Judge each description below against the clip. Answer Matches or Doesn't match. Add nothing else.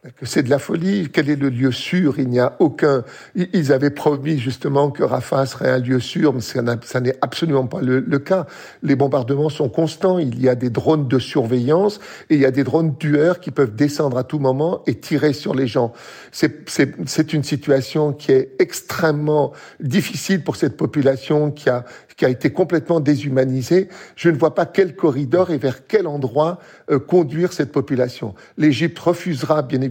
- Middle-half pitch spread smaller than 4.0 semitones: Matches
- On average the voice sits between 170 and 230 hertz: Doesn't match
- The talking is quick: Doesn't match